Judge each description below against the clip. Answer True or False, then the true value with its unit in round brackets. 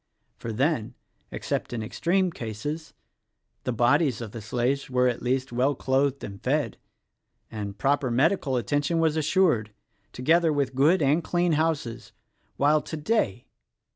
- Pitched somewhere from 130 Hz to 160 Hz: True (135 Hz)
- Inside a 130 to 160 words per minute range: True (155 wpm)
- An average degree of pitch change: True (4.8 semitones)